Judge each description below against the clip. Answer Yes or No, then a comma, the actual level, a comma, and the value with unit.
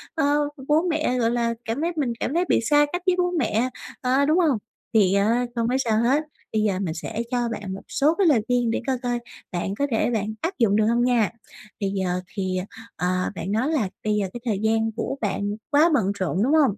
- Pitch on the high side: Yes, high, 235 Hz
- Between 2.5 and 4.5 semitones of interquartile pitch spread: No, average, 5.3 semitones